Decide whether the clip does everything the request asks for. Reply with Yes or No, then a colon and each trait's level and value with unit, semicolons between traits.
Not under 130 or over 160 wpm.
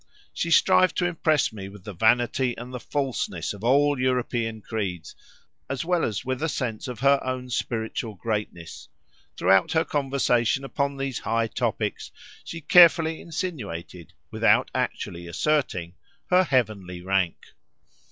Yes: average, 140 wpm